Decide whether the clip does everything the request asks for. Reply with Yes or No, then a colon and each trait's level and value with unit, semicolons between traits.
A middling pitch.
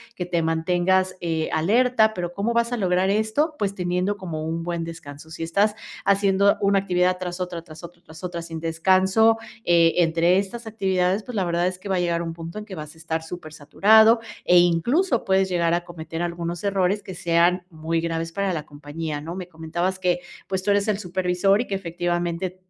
Yes: medium, 180 Hz